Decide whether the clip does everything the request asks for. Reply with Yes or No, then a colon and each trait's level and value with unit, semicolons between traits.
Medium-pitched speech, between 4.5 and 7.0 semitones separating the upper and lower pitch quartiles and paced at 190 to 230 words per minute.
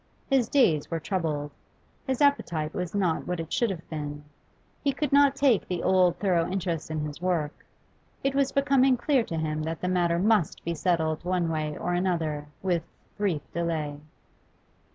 No: medium, 175 Hz; average, 4.9 semitones; average, 175 wpm